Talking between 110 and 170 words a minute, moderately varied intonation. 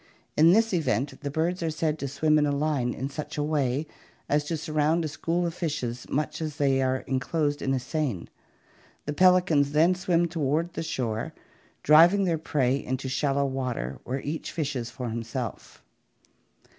No: average, 180 wpm; average, 3.4 semitones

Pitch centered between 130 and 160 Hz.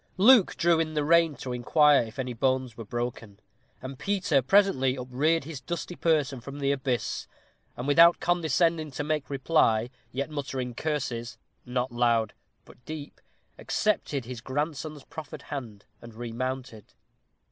Yes: low, 135 Hz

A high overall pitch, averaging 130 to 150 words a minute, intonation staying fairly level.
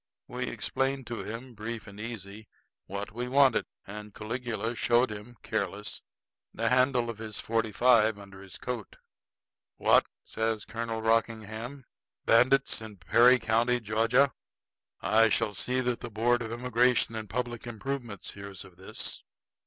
No: low, 115 Hz; average, 145 wpm; narrow, 2.3 semitones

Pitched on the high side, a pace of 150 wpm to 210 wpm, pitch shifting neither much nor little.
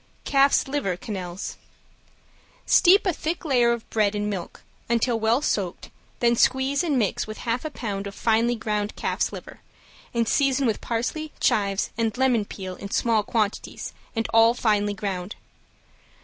Yes: high, 225 Hz; average, 155 wpm; average, 3.9 semitones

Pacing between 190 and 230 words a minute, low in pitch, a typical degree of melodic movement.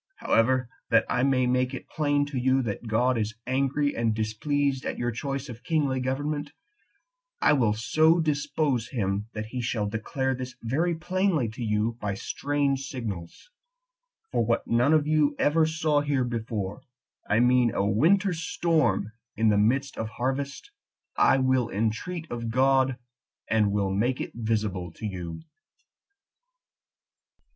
No: average, 150 wpm; low, 125 Hz; average, 4.4 semitones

